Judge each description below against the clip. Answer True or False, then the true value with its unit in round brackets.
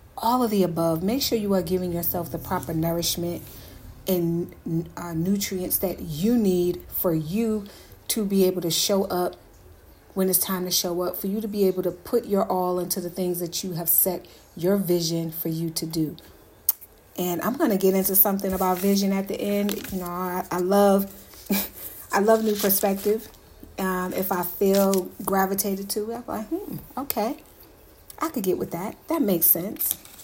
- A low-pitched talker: False (185 Hz)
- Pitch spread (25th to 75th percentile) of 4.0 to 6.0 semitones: False (2.4 semitones)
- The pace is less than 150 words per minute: False (190 wpm)